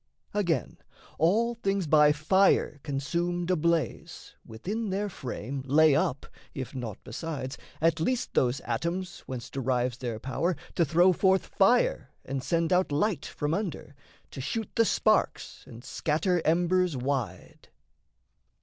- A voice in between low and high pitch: Yes, medium, 160 Hz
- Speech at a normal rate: No, slow, 130 wpm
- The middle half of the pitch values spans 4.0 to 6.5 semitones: Yes, wide, 5.6 semitones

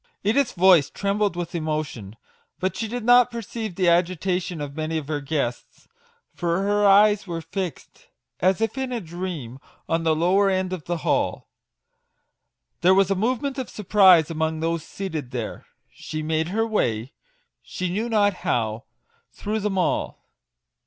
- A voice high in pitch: No, medium, 180 Hz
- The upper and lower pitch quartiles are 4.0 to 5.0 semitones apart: Yes, average, 4.5 semitones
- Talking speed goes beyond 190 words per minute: No, average, 160 wpm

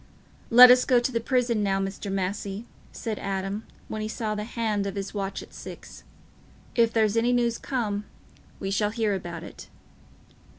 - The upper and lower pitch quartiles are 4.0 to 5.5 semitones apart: No, average, 2.9 semitones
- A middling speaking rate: Yes, average, 175 wpm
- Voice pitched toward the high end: Yes, high, 215 Hz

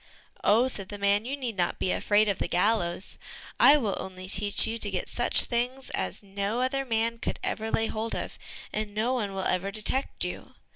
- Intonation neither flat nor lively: Yes, average, 3.0 semitones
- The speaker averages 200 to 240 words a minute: Yes, fast, 205 wpm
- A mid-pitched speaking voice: No, high, 215 Hz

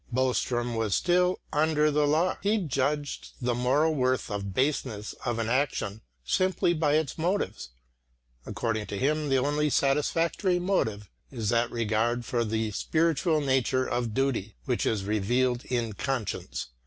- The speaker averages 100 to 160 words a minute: Yes, average, 145 wpm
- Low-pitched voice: Yes, low, 130 Hz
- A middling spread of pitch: Yes, average, 4.9 semitones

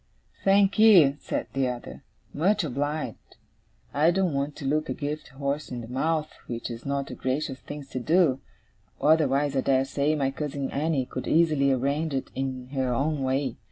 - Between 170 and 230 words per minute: Yes, average, 175 wpm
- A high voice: No, medium, 140 Hz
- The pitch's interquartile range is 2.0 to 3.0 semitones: Yes, narrow, 2.6 semitones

